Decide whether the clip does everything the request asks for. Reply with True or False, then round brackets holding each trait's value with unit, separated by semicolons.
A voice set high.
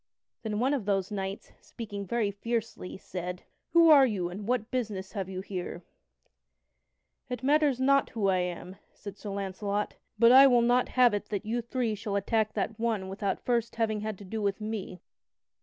True (215 Hz)